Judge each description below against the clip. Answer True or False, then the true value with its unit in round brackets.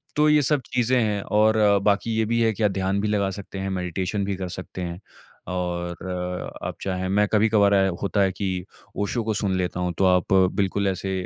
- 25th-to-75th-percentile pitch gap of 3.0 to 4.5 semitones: False (2.4 semitones)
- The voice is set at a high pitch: False (100 Hz)